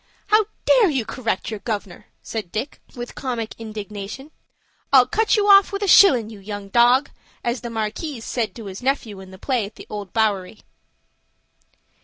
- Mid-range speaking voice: No, high, 230 Hz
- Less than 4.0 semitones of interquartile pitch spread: No, average, 4.3 semitones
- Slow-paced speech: No, average, 175 wpm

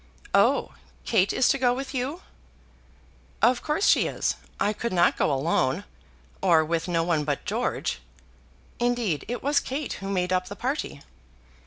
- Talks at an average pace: Yes, average, 160 wpm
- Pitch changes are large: Yes, wide, 6.7 semitones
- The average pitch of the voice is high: Yes, high, 205 Hz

